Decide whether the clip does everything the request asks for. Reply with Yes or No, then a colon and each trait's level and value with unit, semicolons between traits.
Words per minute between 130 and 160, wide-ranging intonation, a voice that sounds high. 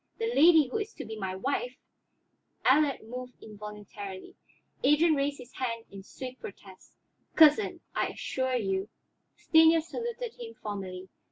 Yes: average, 150 wpm; wide, 7.2 semitones; very high, 255 Hz